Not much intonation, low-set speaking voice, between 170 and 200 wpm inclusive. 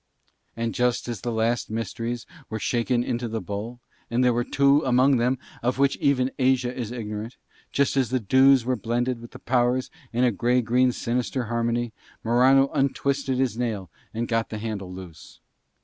Yes: narrow, 2.0 semitones; low, 120 Hz; average, 180 wpm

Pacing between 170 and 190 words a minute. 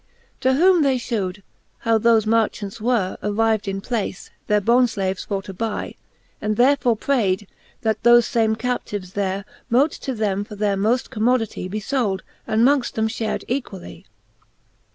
No: average, 155 wpm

